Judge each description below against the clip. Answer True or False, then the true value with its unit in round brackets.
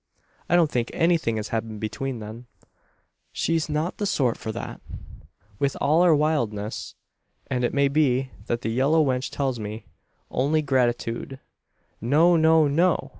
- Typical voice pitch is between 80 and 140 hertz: True (135 Hz)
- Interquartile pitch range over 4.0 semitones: True (5.0 semitones)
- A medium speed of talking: True (150 wpm)